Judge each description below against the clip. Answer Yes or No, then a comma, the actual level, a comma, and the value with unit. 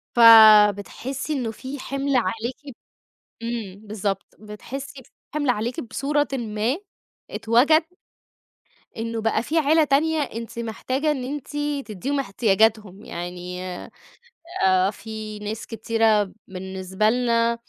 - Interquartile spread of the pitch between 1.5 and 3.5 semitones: No, average, 4.1 semitones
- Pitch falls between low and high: No, high, 225 Hz